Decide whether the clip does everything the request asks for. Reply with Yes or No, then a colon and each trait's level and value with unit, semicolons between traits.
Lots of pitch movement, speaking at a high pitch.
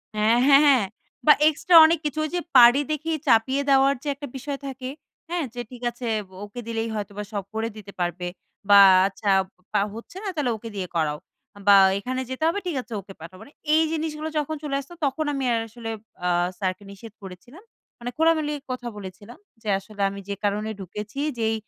Yes: wide, 6.0 semitones; high, 240 Hz